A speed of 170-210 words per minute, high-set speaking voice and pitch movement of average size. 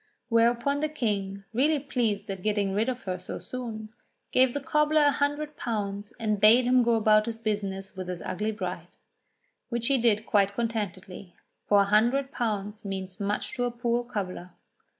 Yes: average, 175 wpm; high, 220 Hz; average, 3.5 semitones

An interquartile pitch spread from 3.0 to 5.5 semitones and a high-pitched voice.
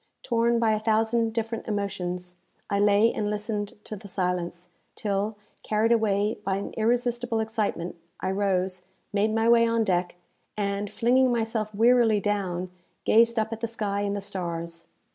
No: narrow, 2.5 semitones; high, 210 Hz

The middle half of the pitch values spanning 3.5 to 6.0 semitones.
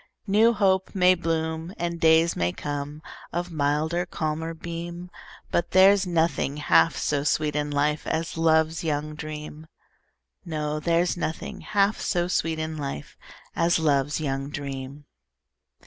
No: narrow, 2.6 semitones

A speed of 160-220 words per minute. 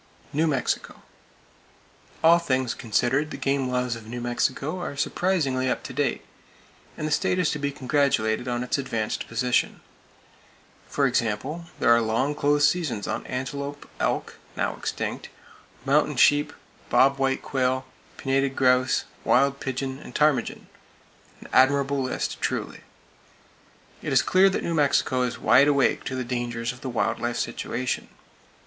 No: average, 145 wpm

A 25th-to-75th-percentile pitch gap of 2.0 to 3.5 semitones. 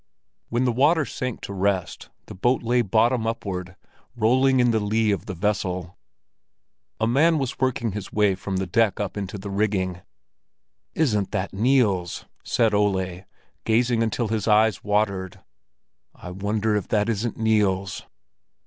Yes: average, 3.2 semitones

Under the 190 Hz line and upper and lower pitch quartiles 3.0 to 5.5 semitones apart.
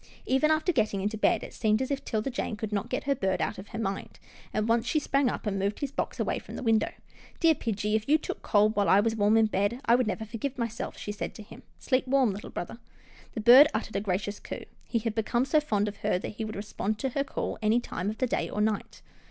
No: high, 220 Hz; average, 3.6 semitones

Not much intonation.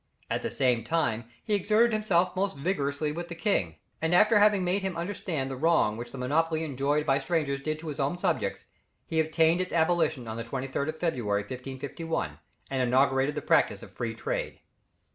No: average, 4.8 semitones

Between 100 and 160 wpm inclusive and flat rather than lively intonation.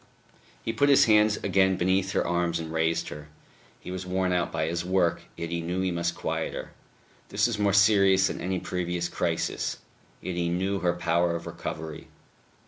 No: average, 190 wpm; narrow, 2.0 semitones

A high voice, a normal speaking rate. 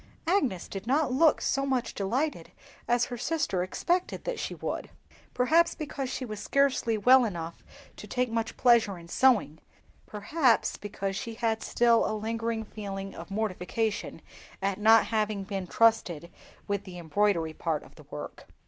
Yes: high, 220 Hz; average, 155 wpm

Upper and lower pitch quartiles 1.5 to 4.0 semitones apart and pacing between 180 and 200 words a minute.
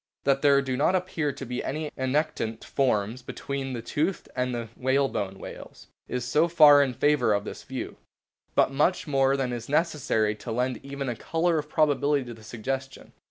Yes: average, 3.2 semitones; average, 190 wpm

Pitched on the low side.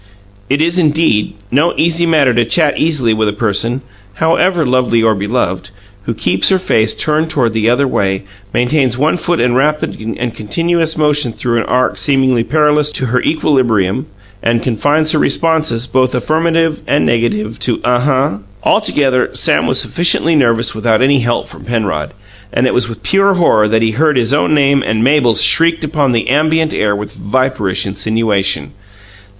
Yes: low, 130 Hz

